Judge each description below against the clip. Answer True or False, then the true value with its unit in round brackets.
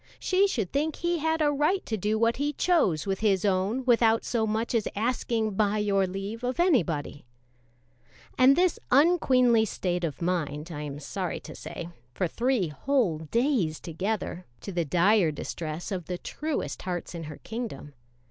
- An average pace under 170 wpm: False (175 wpm)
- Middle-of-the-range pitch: False (215 Hz)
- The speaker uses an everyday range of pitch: False (6.5 semitones)